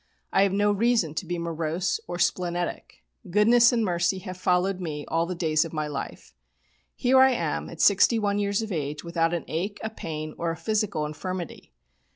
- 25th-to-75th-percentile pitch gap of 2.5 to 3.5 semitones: No, average, 3.9 semitones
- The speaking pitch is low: No, medium, 180 Hz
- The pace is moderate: Yes, average, 190 wpm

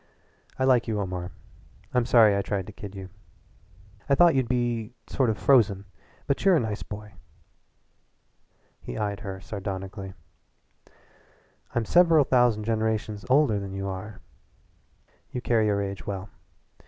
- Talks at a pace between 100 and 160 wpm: Yes, average, 140 wpm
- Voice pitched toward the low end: Yes, low, 105 Hz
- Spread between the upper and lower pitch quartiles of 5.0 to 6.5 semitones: No, average, 3.7 semitones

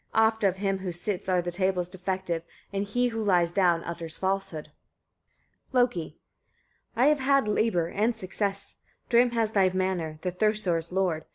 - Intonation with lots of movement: No, average, 3.7 semitones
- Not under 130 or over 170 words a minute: Yes, average, 165 wpm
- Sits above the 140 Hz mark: Yes, high, 190 Hz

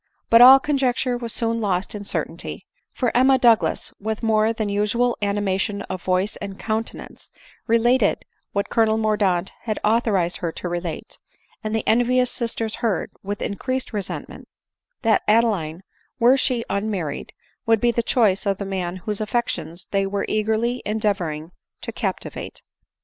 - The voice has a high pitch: Yes, high, 215 Hz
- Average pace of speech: Yes, average, 155 wpm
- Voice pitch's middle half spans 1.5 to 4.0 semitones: Yes, average, 3.0 semitones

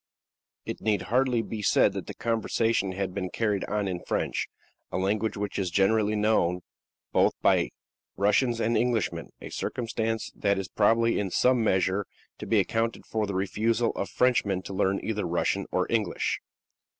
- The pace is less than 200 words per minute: Yes, average, 170 wpm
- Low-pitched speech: Yes, low, 105 Hz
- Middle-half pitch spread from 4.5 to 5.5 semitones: No, average, 2.8 semitones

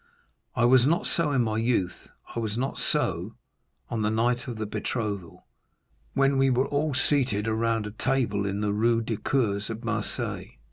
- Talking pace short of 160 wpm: No, average, 180 wpm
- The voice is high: No, low, 115 Hz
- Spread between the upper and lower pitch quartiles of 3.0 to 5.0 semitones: Yes, average, 3.5 semitones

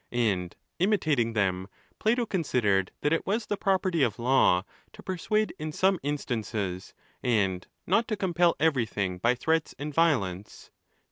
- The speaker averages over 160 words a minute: No, average, 145 wpm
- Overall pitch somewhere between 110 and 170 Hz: Yes, medium, 140 Hz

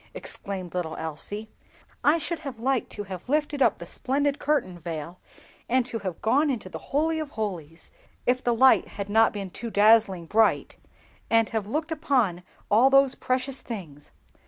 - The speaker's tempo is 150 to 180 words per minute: Yes, average, 160 wpm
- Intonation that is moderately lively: No, wide, 6.4 semitones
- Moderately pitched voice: No, high, 225 Hz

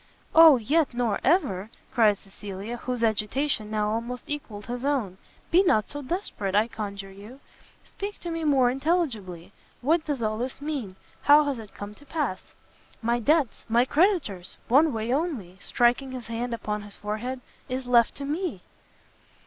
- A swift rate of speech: No, average, 165 wpm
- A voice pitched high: Yes, high, 240 Hz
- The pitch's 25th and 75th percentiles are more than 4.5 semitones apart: Yes, wide, 5.5 semitones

